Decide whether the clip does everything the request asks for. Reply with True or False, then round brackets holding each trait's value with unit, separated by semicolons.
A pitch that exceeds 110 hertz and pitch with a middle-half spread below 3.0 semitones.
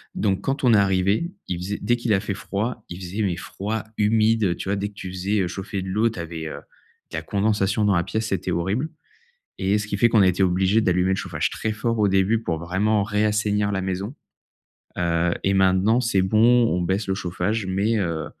False (100 Hz; 2.5 semitones)